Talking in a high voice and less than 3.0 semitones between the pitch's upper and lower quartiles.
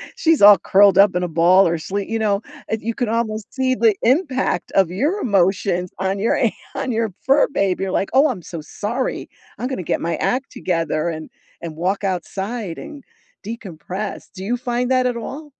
No: high, 205 Hz; average, 5.2 semitones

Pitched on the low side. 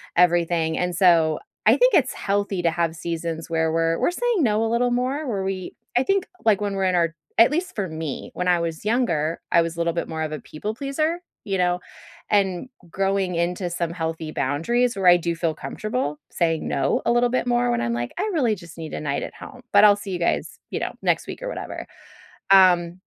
No: medium, 180 Hz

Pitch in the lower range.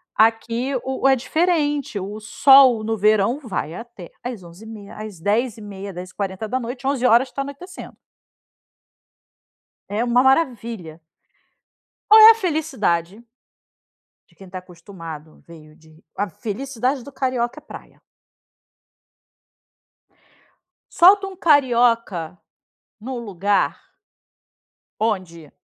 No: high, 225 Hz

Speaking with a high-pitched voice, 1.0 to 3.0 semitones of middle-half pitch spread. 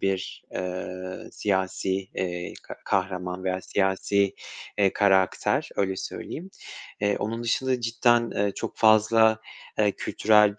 No: low, 100 Hz; narrow, 2.6 semitones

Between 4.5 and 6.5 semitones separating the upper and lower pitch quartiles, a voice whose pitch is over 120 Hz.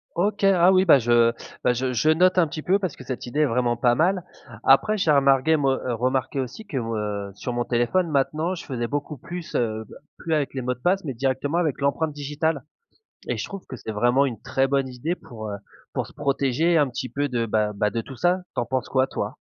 Yes: average, 4.8 semitones; low, 135 Hz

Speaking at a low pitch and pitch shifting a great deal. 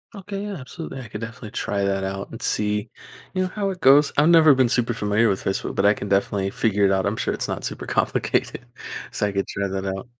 Yes: low, 105 Hz; wide, 6.4 semitones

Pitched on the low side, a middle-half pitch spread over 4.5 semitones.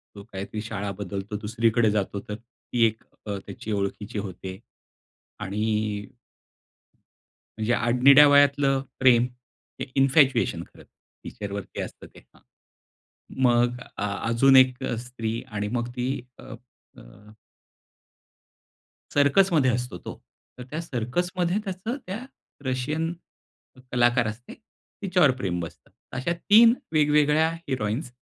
Yes: low, 120 Hz; average, 5.2 semitones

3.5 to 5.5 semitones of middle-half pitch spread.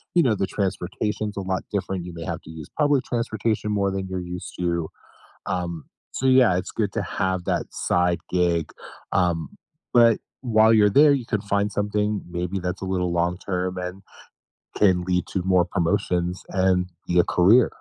No: average, 2.8 semitones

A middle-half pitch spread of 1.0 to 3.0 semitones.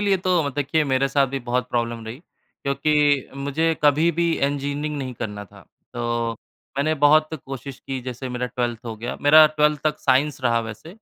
No: average, 3.7 semitones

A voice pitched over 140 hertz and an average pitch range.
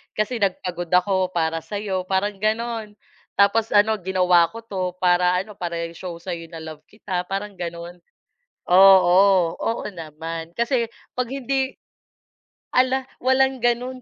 Yes: high, 190 Hz; average, 4.4 semitones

